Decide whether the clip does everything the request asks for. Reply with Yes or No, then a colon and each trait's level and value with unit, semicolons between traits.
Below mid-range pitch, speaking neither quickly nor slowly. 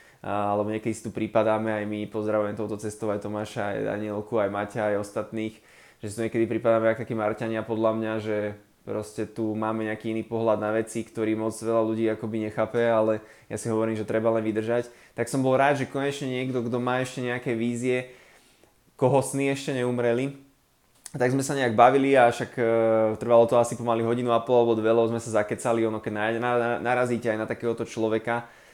No: low, 115 Hz; fast, 195 wpm